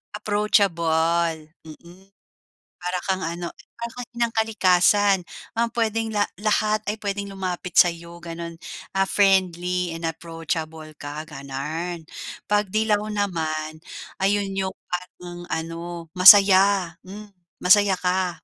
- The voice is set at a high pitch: No, medium, 180 Hz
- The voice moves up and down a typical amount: Yes, average, 3.4 semitones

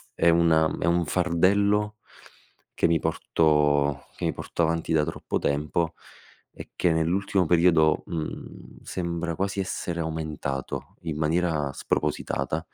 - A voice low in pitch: Yes, very low, 85 Hz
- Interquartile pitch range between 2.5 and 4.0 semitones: No, narrow, 2.1 semitones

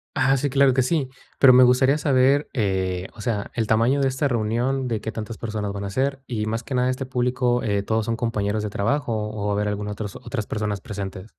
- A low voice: Yes, low, 115 Hz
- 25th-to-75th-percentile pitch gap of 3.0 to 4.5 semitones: Yes, average, 3.8 semitones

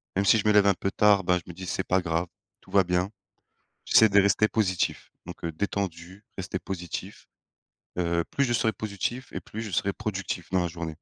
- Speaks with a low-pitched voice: Yes, very low, 95 Hz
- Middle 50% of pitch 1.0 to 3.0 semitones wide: Yes, average, 2.7 semitones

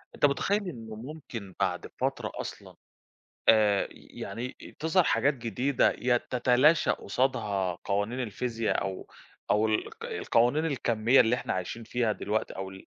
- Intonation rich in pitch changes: No, average, 3.8 semitones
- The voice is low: Yes, low, 115 Hz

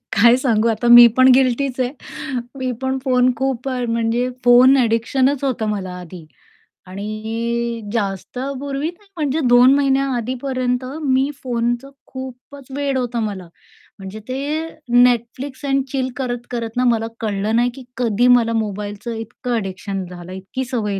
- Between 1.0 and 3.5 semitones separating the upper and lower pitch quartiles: Yes, average, 2.8 semitones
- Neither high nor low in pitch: No, high, 245 Hz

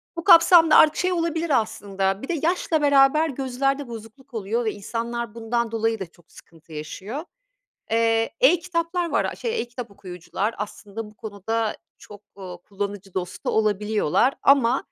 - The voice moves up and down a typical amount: No, wide, 5.7 semitones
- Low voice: No, high, 230 Hz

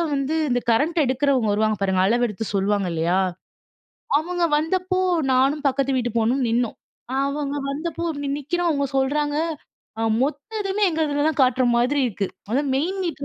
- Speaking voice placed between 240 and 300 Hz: Yes, very high, 275 Hz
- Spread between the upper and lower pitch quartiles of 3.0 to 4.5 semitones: Yes, average, 4.2 semitones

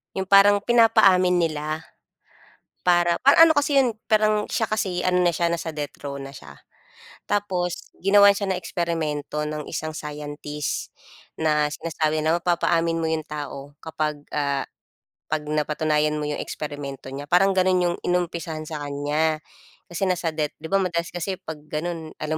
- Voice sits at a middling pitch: Yes, medium, 165 Hz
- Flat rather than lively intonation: No, average, 3.3 semitones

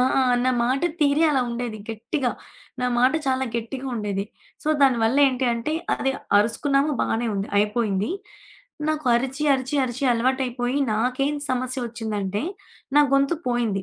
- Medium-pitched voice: No, very high, 250 Hz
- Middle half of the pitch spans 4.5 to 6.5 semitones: No, average, 3.2 semitones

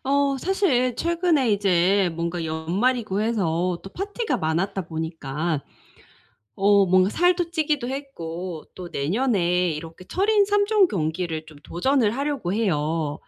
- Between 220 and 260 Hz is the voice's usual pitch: No, high, 195 Hz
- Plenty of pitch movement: Yes, wide, 8.7 semitones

